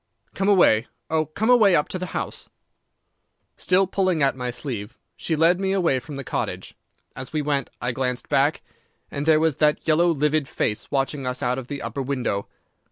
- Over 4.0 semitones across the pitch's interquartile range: Yes, average, 4.6 semitones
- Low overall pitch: No, medium, 150 Hz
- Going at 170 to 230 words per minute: Yes, average, 185 wpm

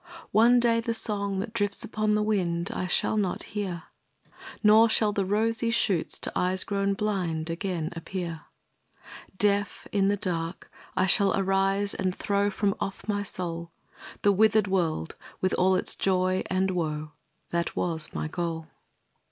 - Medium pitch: No, high, 195 Hz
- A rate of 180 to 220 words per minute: No, average, 155 wpm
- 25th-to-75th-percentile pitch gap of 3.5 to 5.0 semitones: No, average, 2.9 semitones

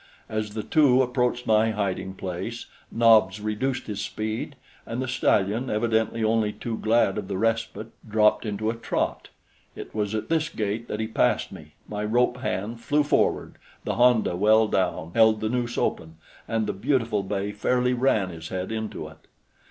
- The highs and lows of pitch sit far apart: No, narrow, 2.5 semitones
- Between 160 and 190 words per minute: Yes, average, 175 wpm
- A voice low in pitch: Yes, low, 110 Hz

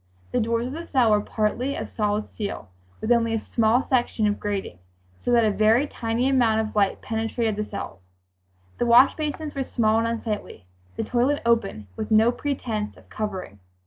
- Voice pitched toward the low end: No, high, 225 Hz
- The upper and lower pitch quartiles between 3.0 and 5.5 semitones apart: No, narrow, 2.4 semitones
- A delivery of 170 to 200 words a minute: Yes, average, 185 wpm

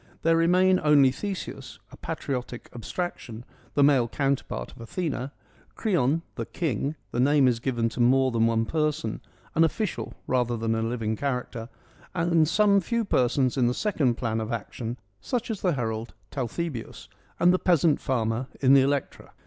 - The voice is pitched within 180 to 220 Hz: No, low, 135 Hz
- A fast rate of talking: No, average, 175 wpm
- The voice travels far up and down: Yes, wide, 5.7 semitones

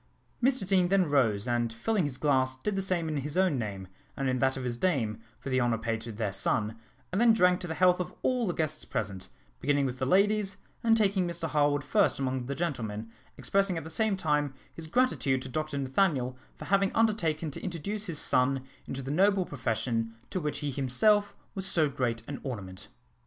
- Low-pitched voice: No, medium, 145 Hz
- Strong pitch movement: Yes, wide, 6.6 semitones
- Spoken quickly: Yes, fast, 210 wpm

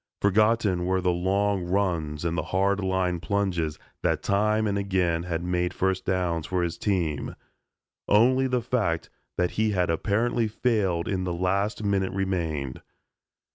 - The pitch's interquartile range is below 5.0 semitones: Yes, narrow, 2.5 semitones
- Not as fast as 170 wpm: Yes, average, 150 wpm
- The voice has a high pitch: No, very low, 95 Hz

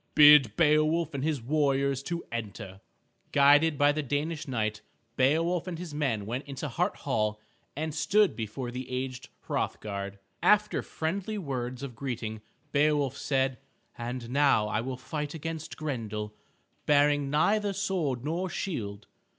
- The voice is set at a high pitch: No, medium, 140 Hz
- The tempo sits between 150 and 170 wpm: No, average, 140 wpm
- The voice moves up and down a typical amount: Yes, average, 4.4 semitones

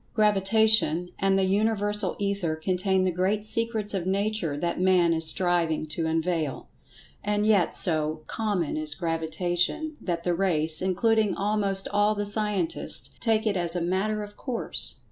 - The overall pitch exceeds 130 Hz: Yes, high, 190 Hz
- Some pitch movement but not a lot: Yes, average, 3.6 semitones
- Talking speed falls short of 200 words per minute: Yes, average, 150 wpm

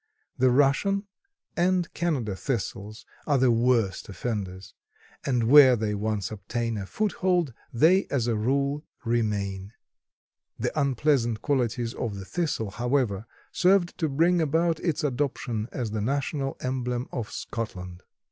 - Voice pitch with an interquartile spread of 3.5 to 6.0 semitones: Yes, average, 5.2 semitones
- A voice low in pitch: Yes, low, 125 Hz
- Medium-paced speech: No, slow, 130 wpm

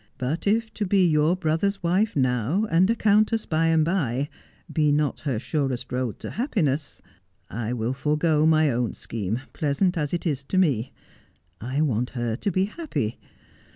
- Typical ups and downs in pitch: No, wide, 6.4 semitones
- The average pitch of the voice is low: No, medium, 150 Hz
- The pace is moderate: Yes, average, 170 wpm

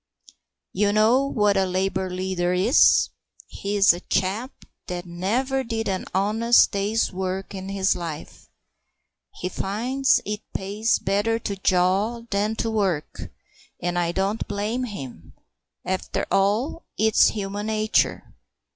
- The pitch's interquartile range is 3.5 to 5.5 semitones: No, average, 2.8 semitones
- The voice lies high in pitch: Yes, high, 200 Hz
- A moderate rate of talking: No, slow, 130 wpm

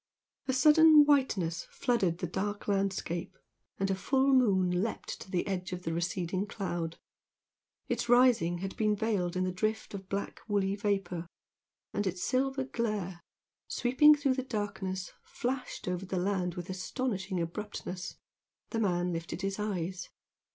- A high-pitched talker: Yes, high, 195 Hz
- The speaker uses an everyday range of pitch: Yes, average, 4.2 semitones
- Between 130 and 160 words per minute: Yes, average, 150 wpm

